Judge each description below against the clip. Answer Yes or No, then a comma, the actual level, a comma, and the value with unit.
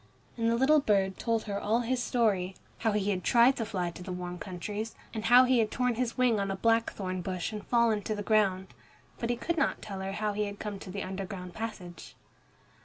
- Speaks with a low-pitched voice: No, high, 210 Hz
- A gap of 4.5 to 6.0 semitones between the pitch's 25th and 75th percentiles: No, average, 3.3 semitones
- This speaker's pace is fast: Yes, fast, 230 wpm